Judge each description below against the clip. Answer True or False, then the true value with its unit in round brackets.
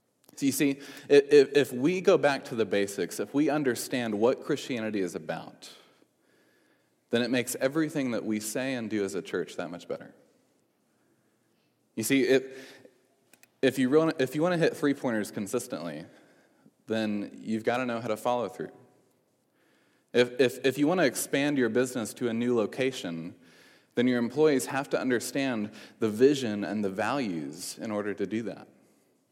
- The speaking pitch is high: False (125 Hz)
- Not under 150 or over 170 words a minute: True (155 wpm)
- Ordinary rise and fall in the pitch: True (3.7 semitones)